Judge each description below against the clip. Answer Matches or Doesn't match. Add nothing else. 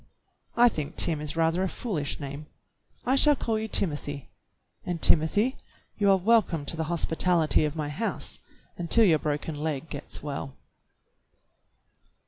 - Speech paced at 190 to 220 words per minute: Doesn't match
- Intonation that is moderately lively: Matches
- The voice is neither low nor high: Matches